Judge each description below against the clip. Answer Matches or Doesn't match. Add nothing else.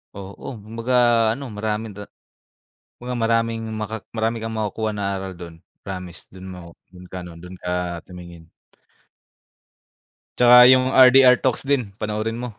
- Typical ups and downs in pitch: Matches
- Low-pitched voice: Matches